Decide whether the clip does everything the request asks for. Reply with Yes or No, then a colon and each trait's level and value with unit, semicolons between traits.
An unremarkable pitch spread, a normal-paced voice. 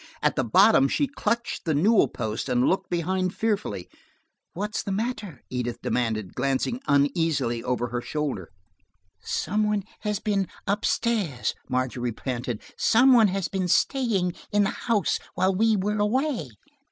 No: wide, 8.6 semitones; average, 145 wpm